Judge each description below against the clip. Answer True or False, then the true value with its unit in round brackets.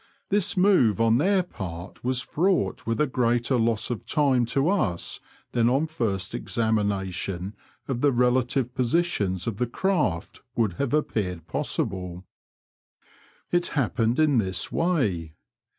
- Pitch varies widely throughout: True (6.5 semitones)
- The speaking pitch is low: True (120 Hz)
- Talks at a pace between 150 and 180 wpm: False (135 wpm)